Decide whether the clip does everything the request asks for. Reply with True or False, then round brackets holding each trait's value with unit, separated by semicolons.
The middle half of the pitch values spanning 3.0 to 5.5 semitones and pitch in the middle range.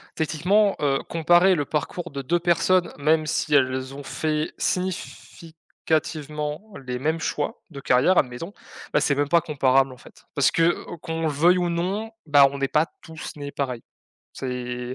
True (3.6 semitones; 155 Hz)